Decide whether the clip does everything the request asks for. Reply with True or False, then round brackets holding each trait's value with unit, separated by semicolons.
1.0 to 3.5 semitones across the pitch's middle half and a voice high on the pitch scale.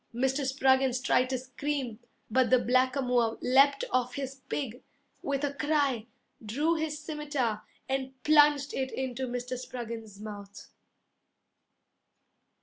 True (2.4 semitones; 260 Hz)